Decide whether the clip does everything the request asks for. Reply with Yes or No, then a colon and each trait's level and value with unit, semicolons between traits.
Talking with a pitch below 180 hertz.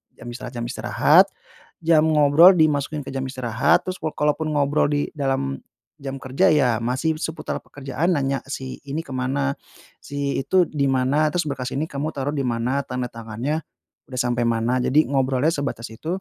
Yes: medium, 140 Hz